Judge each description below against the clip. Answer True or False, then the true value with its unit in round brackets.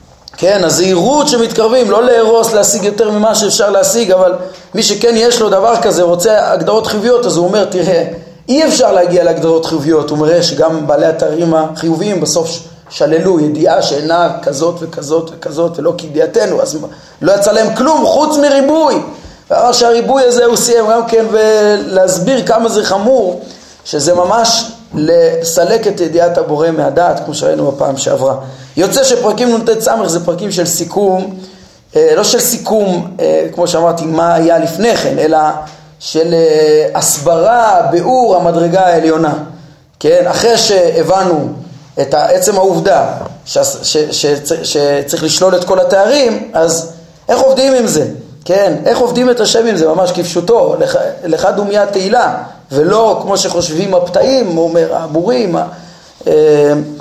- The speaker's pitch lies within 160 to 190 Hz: True (185 Hz)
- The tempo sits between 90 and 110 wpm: False (140 wpm)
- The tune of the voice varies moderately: False (5.7 semitones)